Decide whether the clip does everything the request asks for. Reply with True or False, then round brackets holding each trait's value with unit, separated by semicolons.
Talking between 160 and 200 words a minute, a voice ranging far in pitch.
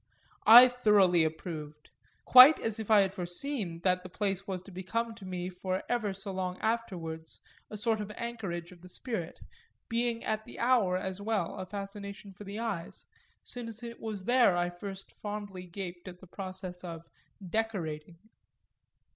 False (165 wpm; 3.7 semitones)